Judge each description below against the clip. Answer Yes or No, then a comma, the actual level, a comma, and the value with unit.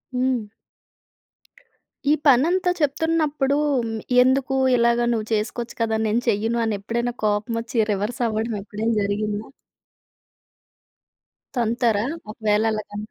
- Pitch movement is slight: No, average, 3.0 semitones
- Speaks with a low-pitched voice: No, high, 230 Hz